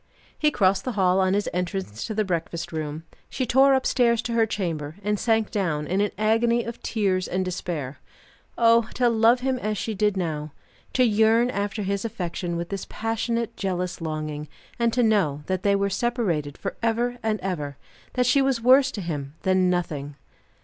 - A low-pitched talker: No, high, 200 Hz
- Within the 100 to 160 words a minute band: No, average, 185 wpm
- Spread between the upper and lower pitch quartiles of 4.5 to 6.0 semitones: Yes, average, 5.0 semitones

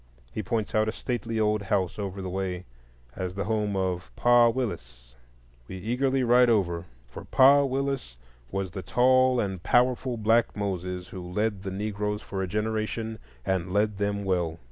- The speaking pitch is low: Yes, low, 105 Hz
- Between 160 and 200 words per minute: Yes, average, 165 wpm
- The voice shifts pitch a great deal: No, average, 3.8 semitones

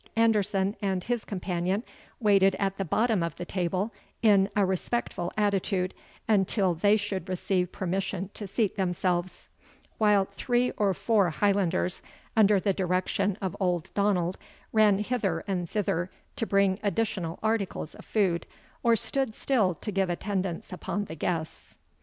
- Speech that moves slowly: No, average, 145 wpm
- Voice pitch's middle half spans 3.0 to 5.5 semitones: No, narrow, 2.4 semitones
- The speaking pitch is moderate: No, high, 195 Hz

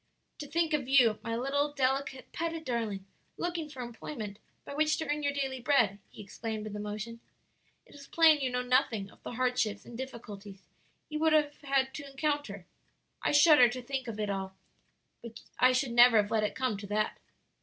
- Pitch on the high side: Yes, very high, 255 Hz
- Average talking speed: Yes, average, 195 wpm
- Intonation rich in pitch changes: No, average, 5.0 semitones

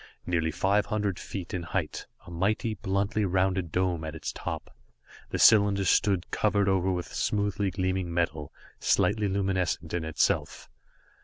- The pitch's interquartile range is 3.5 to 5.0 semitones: No, average, 2.7 semitones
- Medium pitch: No, very low, 95 Hz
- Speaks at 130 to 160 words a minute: Yes, average, 145 wpm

